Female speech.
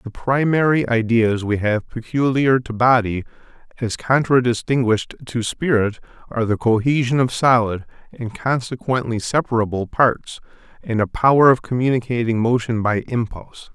No: male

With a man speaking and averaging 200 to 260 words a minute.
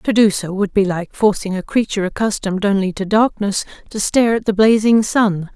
No: female; fast, 205 wpm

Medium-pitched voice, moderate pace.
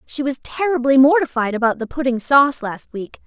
No: very high, 265 Hz; average, 185 wpm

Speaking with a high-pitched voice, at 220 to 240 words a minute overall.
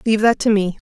No: high, 210 Hz; fast, 275 wpm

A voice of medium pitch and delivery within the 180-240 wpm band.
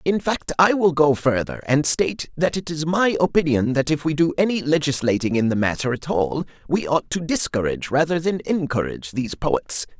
Yes: medium, 150 Hz; average, 200 wpm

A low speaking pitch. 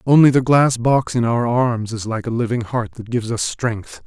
Yes: low, 120 Hz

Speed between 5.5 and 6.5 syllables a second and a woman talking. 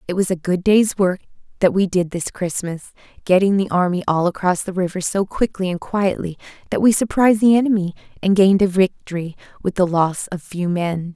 Yes: 5.6 syllables/s; female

